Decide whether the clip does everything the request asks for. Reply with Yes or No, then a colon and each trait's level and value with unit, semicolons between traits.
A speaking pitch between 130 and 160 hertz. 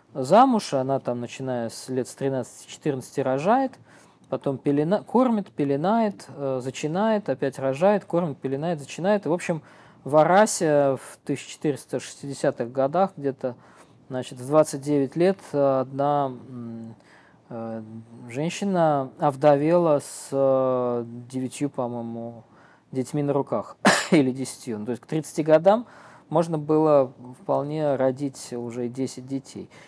Yes: medium, 140 Hz